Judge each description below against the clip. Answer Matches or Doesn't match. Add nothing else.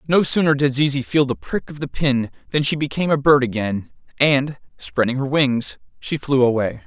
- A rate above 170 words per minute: Matches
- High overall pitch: Doesn't match